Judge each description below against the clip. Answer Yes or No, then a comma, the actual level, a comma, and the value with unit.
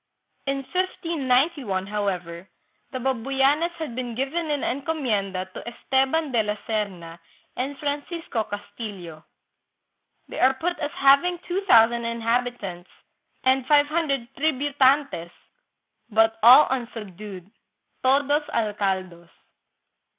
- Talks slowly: Yes, slow, 110 wpm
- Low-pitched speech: No, very high, 255 Hz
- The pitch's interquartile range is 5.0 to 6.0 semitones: Yes, wide, 5.5 semitones